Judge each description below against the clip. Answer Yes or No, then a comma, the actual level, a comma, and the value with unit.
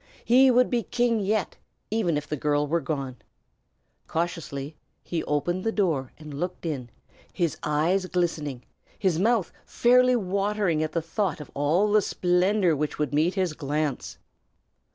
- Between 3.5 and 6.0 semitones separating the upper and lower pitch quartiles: Yes, average, 5.3 semitones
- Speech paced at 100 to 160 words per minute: Yes, average, 155 wpm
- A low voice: No, medium, 170 Hz